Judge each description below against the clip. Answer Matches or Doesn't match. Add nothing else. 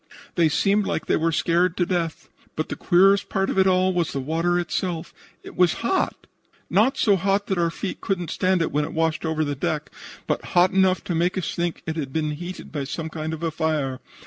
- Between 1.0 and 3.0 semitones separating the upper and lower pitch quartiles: Matches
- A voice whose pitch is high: Doesn't match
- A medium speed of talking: Doesn't match